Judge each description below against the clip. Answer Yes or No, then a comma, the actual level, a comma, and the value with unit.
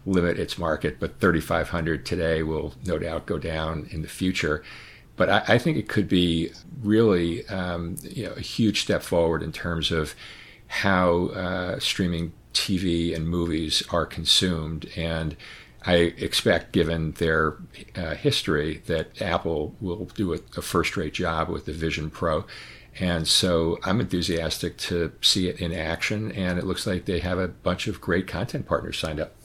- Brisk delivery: No, average, 165 wpm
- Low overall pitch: Yes, very low, 85 Hz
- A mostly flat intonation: Yes, narrow, 2.2 semitones